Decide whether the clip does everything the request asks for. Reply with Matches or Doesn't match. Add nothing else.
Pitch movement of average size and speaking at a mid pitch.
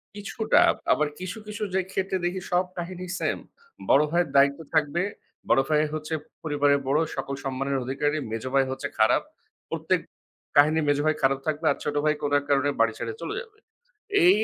Matches